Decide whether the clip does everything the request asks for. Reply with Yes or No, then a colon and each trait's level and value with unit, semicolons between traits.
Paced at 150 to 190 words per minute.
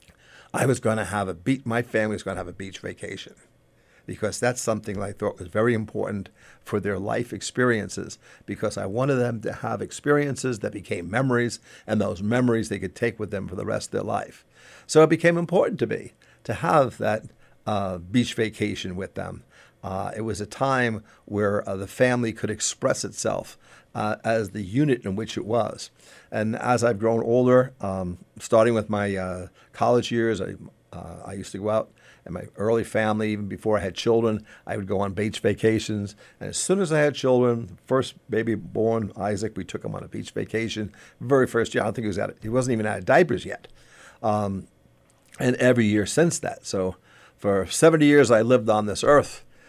No: fast, 205 wpm